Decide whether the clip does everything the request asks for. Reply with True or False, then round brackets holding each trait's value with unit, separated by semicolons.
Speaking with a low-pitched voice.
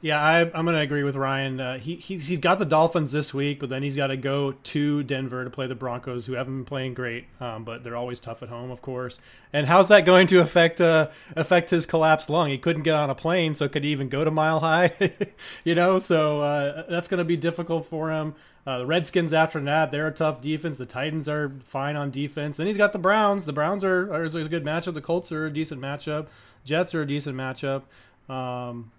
False (155 Hz)